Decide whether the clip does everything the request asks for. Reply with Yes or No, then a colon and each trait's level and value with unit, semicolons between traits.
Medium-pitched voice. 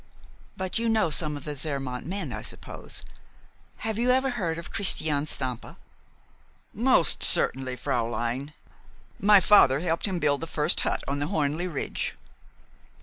Yes: medium, 155 Hz